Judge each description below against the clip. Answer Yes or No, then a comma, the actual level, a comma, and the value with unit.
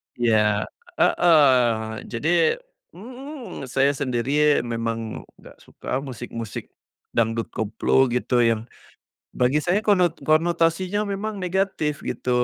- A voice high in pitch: No, low, 135 Hz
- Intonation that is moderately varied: No, wide, 7.2 semitones